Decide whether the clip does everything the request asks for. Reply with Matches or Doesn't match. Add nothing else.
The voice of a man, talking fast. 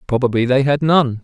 Doesn't match